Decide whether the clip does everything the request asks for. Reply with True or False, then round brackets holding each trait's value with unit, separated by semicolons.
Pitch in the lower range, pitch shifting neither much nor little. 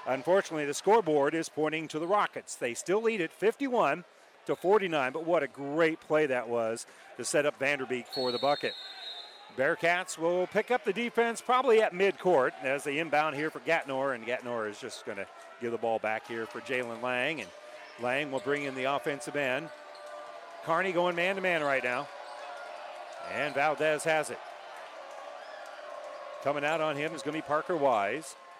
False (150 Hz; 4.8 semitones)